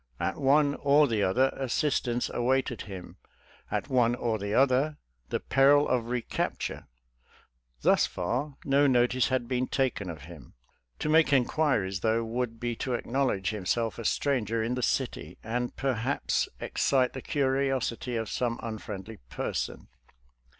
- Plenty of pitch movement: No, average, 3.2 semitones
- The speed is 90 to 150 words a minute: Yes, average, 145 wpm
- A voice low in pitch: Yes, low, 125 Hz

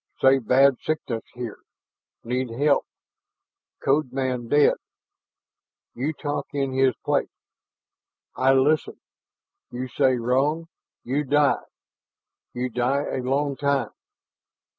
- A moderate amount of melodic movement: No, narrow, 2.3 semitones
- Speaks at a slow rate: Yes, slow, 105 wpm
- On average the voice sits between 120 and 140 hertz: Yes, low, 135 Hz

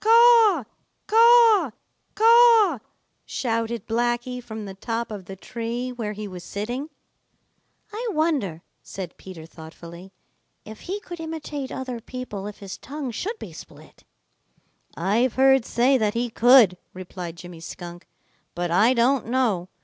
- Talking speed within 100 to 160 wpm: Yes, average, 140 wpm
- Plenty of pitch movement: Yes, wide, 6.6 semitones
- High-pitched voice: Yes, high, 235 Hz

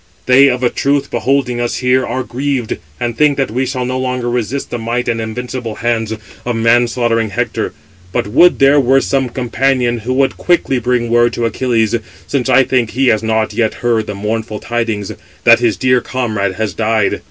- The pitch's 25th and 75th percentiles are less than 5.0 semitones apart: Yes, narrow, 2.4 semitones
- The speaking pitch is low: Yes, low, 120 Hz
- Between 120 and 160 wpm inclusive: No, average, 195 wpm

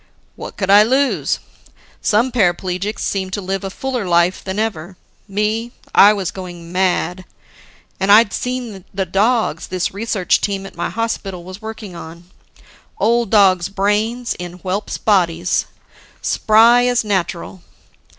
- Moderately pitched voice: No, high, 195 Hz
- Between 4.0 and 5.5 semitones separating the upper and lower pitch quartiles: No, average, 3.2 semitones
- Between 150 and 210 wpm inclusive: No, average, 140 wpm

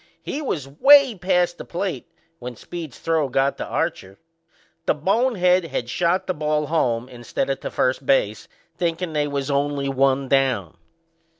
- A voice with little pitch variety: No, average, 4.8 semitones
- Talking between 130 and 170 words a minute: Yes, average, 160 wpm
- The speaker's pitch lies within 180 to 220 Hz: No, medium, 150 Hz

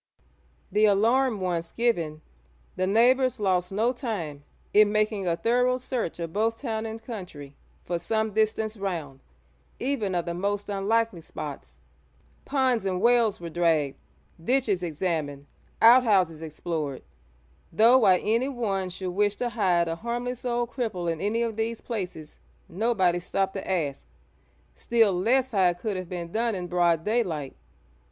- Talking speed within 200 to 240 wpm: No, average, 145 wpm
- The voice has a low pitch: No, high, 200 Hz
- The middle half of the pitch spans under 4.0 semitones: No, average, 4.9 semitones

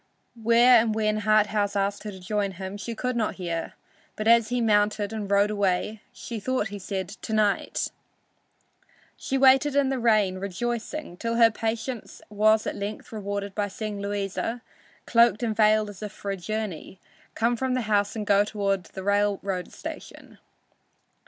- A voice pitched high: Yes, high, 210 Hz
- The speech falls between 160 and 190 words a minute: Yes, average, 170 wpm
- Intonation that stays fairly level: Yes, narrow, 2.2 semitones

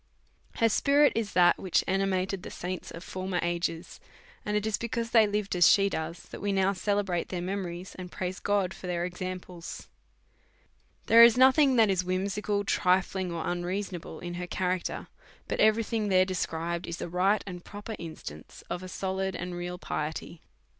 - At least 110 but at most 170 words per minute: No, average, 185 wpm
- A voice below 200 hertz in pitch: Yes, medium, 185 Hz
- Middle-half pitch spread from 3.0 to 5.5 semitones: No, narrow, 2.6 semitones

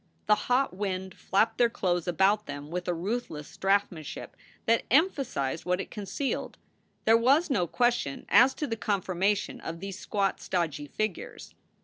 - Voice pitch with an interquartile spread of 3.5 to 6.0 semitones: Yes, average, 4.6 semitones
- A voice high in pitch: Yes, high, 195 Hz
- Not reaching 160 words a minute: Yes, average, 150 wpm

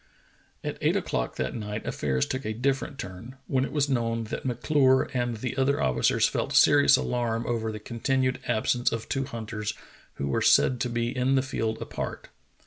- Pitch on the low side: Yes, low, 120 Hz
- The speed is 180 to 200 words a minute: Yes, average, 185 wpm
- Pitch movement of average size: Yes, average, 3.3 semitones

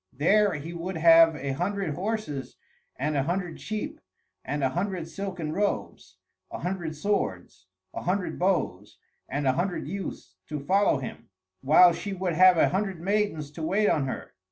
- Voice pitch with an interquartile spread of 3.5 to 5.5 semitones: Yes, average, 4.8 semitones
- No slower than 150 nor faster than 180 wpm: Yes, average, 165 wpm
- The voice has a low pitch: No, medium, 170 Hz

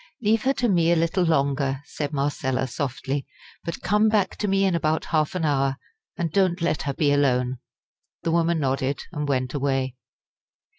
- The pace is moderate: Yes, average, 180 wpm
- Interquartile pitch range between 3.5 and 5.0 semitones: Yes, average, 4.1 semitones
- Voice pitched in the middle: Yes, medium, 150 Hz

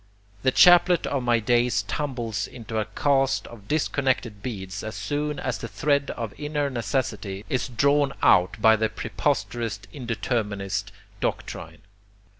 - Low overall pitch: Yes, low, 120 Hz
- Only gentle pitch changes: No, average, 4.5 semitones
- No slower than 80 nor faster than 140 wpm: Yes, slow, 135 wpm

